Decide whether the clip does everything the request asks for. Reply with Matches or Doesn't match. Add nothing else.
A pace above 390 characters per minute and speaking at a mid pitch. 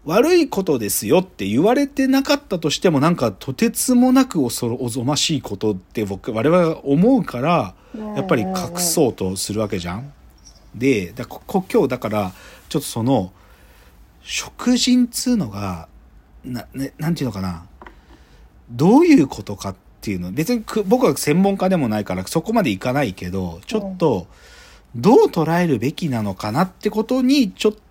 Doesn't match